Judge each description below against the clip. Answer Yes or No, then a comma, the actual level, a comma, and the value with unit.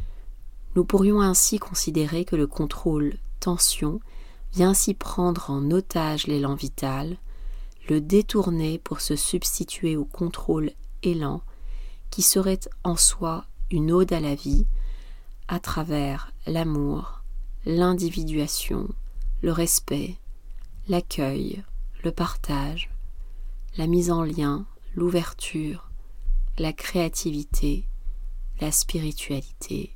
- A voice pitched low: No, medium, 155 Hz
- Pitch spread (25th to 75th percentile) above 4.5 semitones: No, average, 4.2 semitones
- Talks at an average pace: No, slow, 100 wpm